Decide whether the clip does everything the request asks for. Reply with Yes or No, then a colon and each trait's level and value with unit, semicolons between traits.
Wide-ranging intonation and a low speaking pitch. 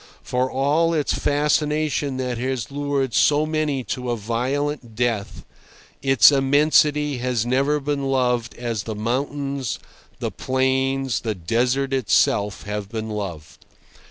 No: average, 3.5 semitones; low, 130 Hz